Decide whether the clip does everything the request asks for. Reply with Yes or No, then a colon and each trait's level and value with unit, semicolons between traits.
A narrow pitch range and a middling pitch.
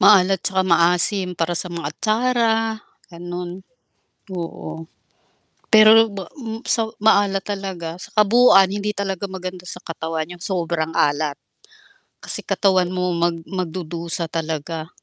No: average, 3.0 semitones; medium, 180 Hz